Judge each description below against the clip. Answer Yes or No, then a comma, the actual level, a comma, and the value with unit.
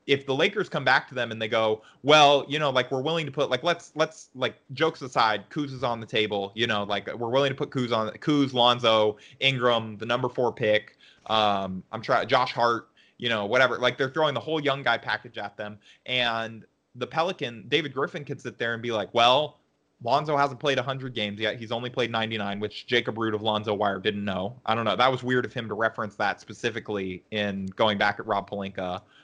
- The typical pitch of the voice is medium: No, low, 120 Hz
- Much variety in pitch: No, average, 4.1 semitones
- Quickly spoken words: Yes, fast, 230 wpm